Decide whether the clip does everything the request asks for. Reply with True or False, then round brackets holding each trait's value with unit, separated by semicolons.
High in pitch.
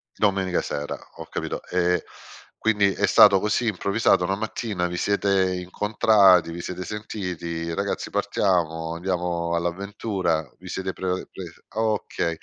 False (95 Hz)